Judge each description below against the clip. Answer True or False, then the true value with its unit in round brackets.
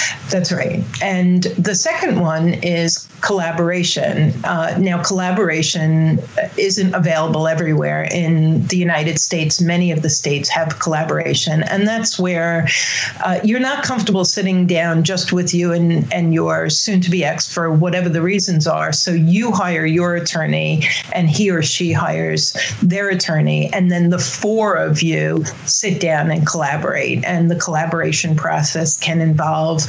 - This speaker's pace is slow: False (155 wpm)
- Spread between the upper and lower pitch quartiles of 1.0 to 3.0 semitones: True (2.4 semitones)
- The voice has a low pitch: False (170 Hz)